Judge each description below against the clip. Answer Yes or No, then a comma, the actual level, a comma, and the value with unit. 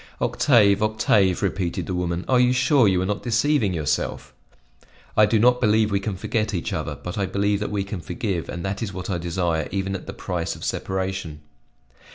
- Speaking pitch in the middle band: No, low, 100 Hz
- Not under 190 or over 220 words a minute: Yes, fast, 205 wpm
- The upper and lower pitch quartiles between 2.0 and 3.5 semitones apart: Yes, average, 3.1 semitones